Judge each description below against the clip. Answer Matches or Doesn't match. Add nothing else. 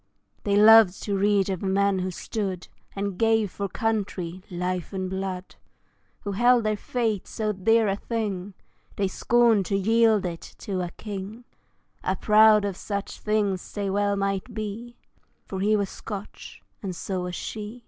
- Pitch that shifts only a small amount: Matches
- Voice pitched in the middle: Doesn't match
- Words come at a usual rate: Matches